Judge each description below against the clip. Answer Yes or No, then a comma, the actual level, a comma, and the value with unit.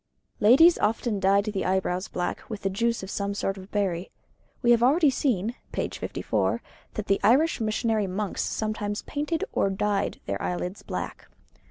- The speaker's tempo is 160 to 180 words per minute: Yes, average, 165 wpm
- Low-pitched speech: No, high, 210 Hz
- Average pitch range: Yes, average, 3.3 semitones